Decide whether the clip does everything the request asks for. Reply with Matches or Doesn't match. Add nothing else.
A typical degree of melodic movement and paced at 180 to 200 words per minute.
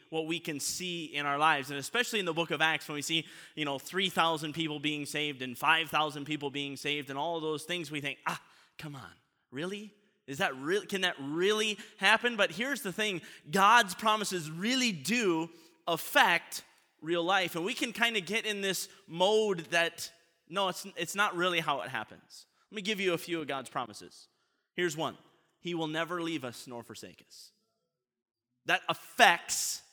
Matches